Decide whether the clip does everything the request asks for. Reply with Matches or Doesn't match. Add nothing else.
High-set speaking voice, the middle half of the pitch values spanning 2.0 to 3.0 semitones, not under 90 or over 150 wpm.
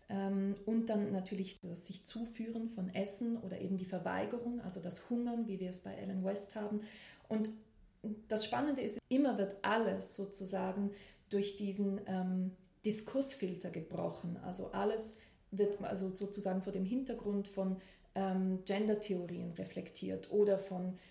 Matches